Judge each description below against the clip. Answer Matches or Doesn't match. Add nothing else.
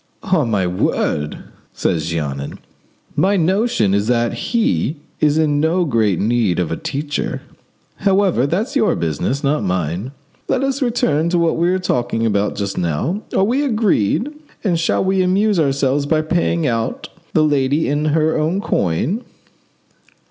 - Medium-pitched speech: Matches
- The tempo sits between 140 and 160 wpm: Matches